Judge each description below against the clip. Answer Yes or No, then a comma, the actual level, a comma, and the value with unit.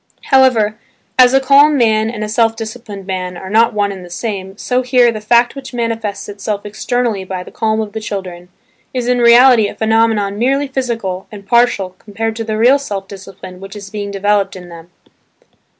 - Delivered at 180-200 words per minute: Yes, average, 195 wpm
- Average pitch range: Yes, average, 3.2 semitones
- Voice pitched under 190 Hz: No, high, 215 Hz